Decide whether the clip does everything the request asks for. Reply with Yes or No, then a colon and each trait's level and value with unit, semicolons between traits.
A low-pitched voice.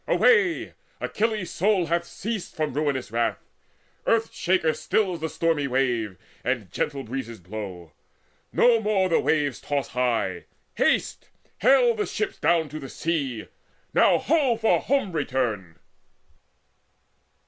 No: medium, 155 Hz